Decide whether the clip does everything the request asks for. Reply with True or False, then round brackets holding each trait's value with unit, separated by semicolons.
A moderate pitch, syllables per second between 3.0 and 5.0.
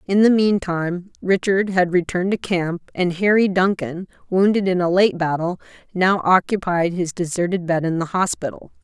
True (180 Hz; 4.9 syllables/s)